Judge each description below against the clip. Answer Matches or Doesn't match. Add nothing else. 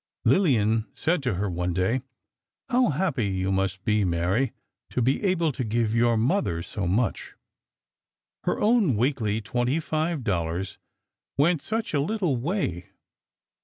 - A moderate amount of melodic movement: Doesn't match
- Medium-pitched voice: Doesn't match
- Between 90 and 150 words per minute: Matches